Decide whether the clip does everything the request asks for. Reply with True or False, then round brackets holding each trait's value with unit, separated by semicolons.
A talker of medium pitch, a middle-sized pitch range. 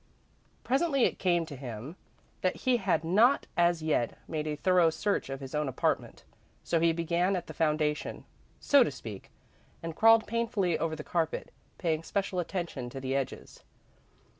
True (165 Hz; 4.0 semitones)